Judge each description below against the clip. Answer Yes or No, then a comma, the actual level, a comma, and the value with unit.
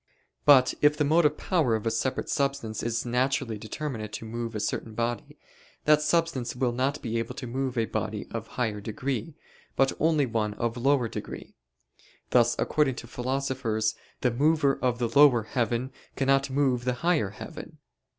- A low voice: Yes, low, 125 Hz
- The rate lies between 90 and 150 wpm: No, average, 170 wpm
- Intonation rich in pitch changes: No, average, 3.4 semitones